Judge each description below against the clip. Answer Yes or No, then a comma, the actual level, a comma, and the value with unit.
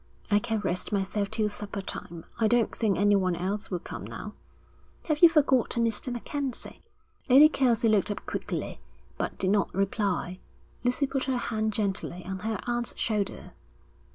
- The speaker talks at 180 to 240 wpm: No, average, 160 wpm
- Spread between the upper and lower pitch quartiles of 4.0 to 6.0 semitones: No, average, 3.6 semitones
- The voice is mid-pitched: No, high, 215 Hz